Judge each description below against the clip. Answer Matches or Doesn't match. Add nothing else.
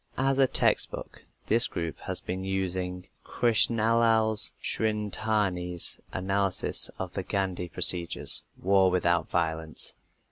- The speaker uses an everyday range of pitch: Matches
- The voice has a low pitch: Matches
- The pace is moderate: Doesn't match